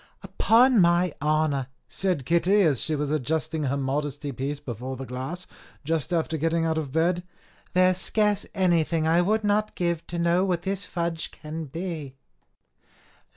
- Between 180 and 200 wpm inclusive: No, average, 160 wpm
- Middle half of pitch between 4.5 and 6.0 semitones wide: No, average, 3.5 semitones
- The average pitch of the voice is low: No, medium, 165 Hz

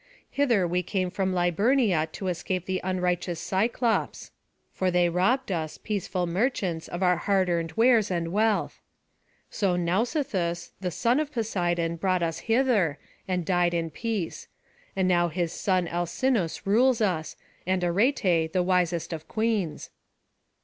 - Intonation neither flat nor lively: Yes, average, 3.8 semitones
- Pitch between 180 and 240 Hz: Yes, medium, 185 Hz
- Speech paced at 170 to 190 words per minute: No, average, 140 wpm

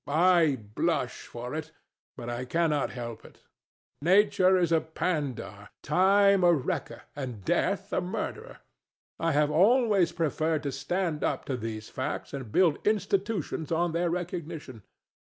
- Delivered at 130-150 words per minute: Yes, average, 140 wpm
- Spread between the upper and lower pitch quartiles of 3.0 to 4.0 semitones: No, average, 4.6 semitones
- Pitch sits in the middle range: Yes, medium, 160 Hz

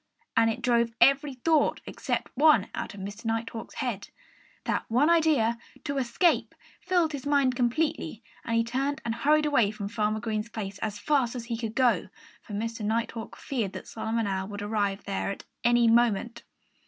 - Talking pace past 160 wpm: Yes, average, 180 wpm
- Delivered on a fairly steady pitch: No, average, 3.8 semitones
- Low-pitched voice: No, high, 230 Hz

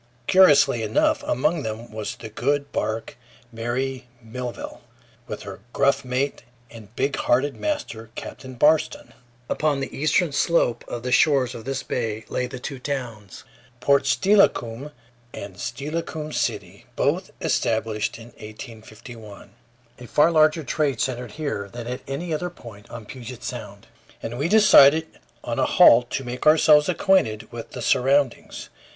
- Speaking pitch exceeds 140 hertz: No, low, 130 Hz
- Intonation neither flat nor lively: Yes, average, 4.5 semitones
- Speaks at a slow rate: No, average, 145 wpm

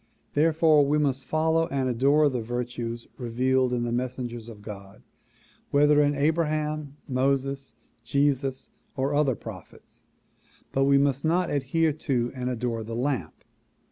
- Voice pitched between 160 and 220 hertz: No, low, 135 Hz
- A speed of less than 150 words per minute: Yes, average, 140 wpm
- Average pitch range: Yes, average, 3.2 semitones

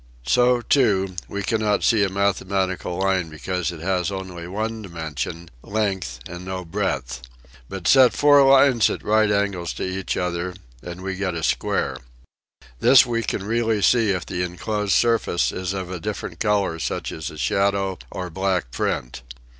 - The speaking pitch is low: Yes, very low, 95 Hz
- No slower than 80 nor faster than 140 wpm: No, average, 170 wpm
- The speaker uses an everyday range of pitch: Yes, average, 3.2 semitones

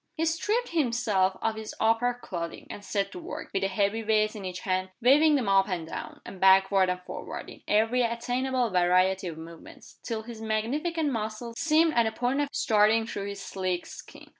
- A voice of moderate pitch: No, high, 220 Hz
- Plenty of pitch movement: No, average, 4.3 semitones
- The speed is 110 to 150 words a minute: No, average, 200 wpm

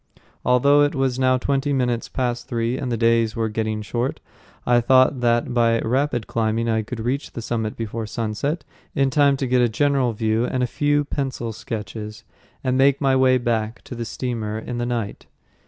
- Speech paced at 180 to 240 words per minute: Yes, average, 190 wpm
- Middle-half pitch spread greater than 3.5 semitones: No, average, 2.7 semitones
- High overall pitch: No, low, 120 Hz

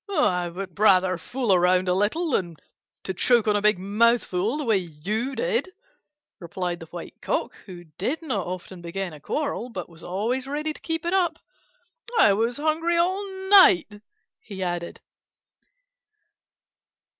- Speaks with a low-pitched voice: No, high, 205 Hz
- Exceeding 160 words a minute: No, average, 155 wpm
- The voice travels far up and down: Yes, wide, 7.9 semitones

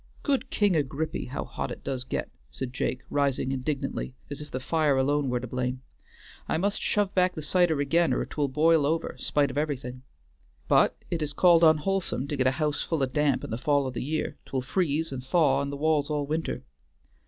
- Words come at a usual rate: No, fast, 220 wpm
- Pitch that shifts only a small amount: No, average, 3.3 semitones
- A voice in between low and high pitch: Yes, medium, 145 Hz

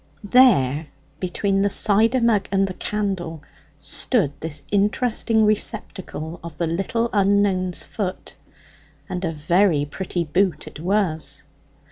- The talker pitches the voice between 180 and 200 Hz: Yes, high, 190 Hz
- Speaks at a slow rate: Yes, slow, 120 wpm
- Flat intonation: No, average, 4.0 semitones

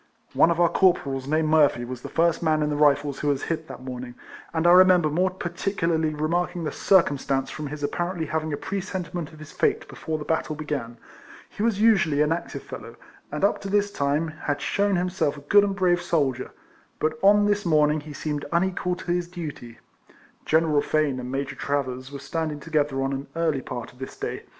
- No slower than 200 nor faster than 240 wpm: Yes, fast, 205 wpm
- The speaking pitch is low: No, medium, 155 Hz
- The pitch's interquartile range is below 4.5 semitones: Yes, average, 3.6 semitones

